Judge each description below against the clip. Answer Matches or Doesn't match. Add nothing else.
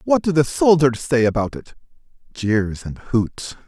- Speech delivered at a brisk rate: Doesn't match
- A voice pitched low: Matches